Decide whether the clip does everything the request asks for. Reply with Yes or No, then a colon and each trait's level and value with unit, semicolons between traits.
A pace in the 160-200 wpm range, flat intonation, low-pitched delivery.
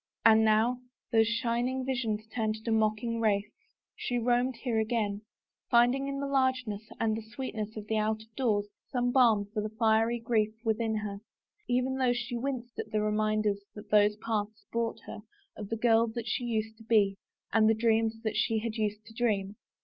No: average, 185 wpm; narrow, 2.0 semitones; high, 225 Hz